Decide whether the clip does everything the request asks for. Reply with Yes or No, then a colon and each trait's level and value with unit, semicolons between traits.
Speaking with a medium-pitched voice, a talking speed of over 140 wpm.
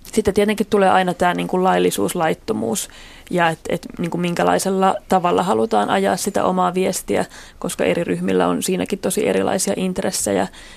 Yes: medium, 180 Hz; average, 150 wpm